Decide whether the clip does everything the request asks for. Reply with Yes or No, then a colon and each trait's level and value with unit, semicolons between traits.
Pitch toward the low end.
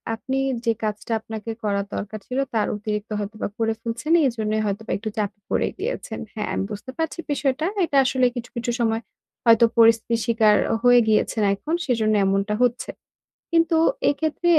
No: high, 225 Hz